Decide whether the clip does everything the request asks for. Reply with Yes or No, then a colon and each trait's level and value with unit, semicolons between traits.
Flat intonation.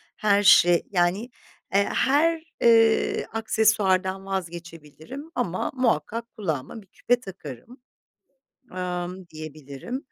No: average, 4.9 semitones